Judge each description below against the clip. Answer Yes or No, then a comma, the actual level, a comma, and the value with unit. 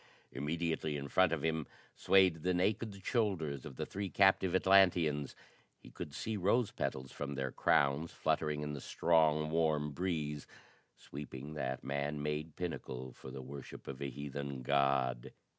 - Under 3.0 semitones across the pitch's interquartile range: No, average, 3.9 semitones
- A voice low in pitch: Yes, very low, 75 Hz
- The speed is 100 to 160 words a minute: Yes, average, 155 wpm